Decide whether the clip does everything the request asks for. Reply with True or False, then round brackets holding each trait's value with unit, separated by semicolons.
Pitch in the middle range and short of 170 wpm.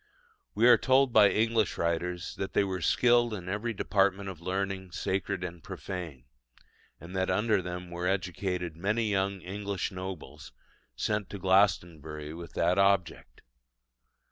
False (95 Hz; 145 wpm)